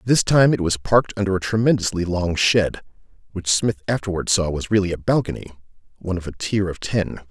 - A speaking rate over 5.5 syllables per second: Yes, 5.8 syllables/s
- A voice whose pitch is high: No, low, 100 Hz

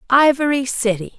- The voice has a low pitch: No, very high, 255 Hz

